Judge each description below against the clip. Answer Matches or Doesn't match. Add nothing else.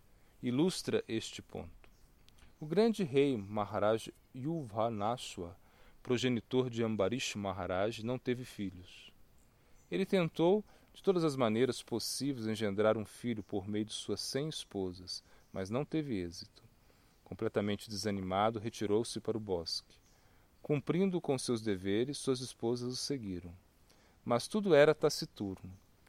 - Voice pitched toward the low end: Matches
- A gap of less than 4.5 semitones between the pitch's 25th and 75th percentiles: Doesn't match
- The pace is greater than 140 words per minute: Doesn't match